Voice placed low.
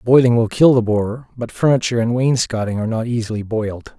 Yes: low, 115 Hz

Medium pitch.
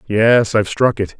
No: low, 105 Hz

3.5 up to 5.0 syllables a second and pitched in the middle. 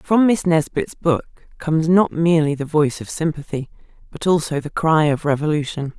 No: 5.2 syllables/s; medium, 155 Hz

